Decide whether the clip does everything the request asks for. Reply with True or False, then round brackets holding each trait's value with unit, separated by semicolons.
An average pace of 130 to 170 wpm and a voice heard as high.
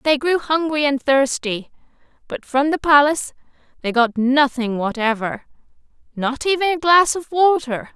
True (145 wpm; 280 Hz)